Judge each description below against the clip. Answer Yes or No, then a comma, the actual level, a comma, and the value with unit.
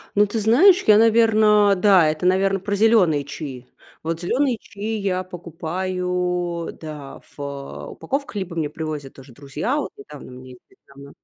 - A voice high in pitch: No, medium, 180 Hz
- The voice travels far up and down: Yes, wide, 5.7 semitones